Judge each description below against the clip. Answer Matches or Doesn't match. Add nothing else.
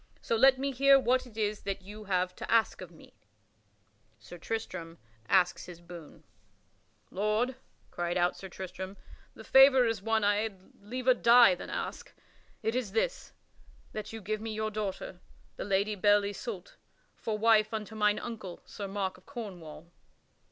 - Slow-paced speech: Doesn't match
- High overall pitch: Matches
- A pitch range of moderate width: Matches